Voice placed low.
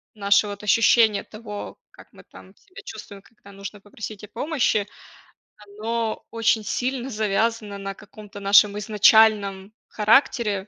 No: high, 210 Hz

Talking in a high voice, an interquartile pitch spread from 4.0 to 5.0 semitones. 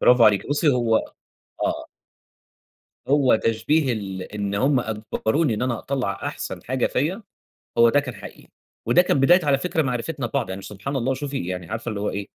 No: low, 125 Hz; average, 4.6 semitones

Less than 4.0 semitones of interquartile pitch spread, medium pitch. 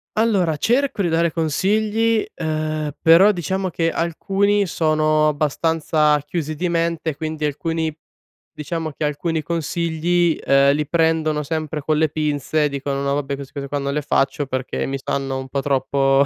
Yes: average, 2.7 semitones; medium, 155 Hz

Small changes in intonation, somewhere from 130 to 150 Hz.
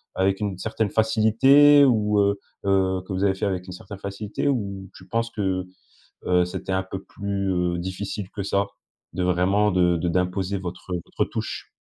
No: narrow, 2.2 semitones; very low, 95 Hz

